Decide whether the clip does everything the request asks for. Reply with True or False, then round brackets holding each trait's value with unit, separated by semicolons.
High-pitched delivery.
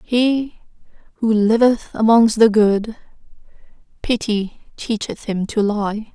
True (220 Hz)